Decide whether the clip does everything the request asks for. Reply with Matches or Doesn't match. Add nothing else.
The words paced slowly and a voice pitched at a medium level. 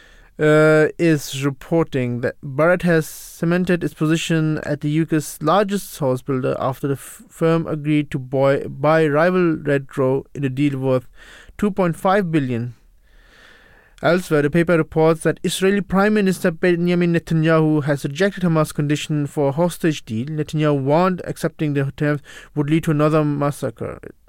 Doesn't match